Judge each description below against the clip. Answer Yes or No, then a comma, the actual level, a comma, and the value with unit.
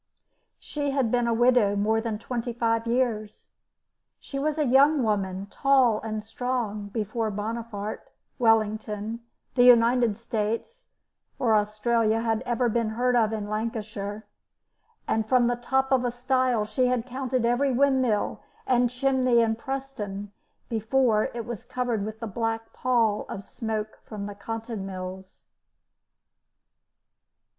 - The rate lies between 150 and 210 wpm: No, slow, 135 wpm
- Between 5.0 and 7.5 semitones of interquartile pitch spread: No, average, 2.7 semitones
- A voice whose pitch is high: Yes, high, 230 Hz